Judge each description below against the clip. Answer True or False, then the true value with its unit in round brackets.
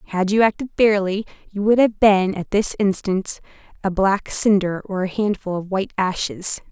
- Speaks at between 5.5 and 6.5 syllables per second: False (4.9 syllables/s)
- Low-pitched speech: False (200 Hz)